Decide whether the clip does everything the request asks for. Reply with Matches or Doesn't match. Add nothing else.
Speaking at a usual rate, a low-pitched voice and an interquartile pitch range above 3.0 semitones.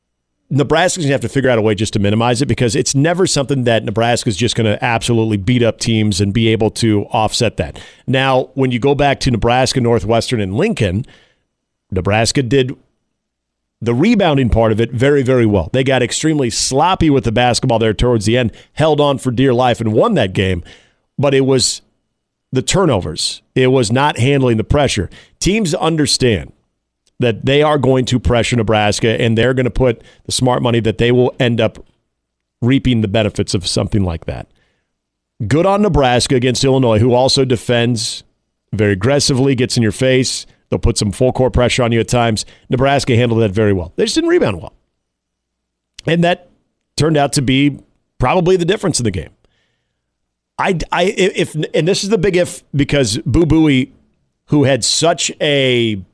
Matches